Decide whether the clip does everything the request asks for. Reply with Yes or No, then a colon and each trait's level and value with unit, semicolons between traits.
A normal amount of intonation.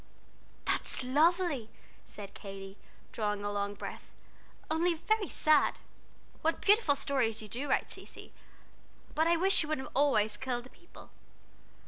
No: wide, 7.5 semitones